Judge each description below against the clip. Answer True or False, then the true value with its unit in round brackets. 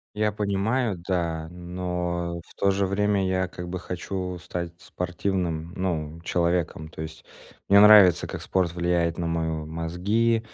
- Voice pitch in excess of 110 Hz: False (90 Hz)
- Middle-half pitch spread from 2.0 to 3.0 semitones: True (2.5 semitones)